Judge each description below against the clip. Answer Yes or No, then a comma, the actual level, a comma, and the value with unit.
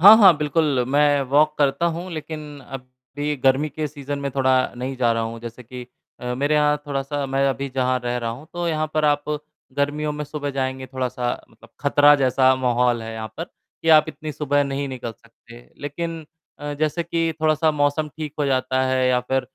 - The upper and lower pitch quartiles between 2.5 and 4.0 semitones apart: Yes, average, 2.9 semitones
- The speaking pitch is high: No, medium, 140 Hz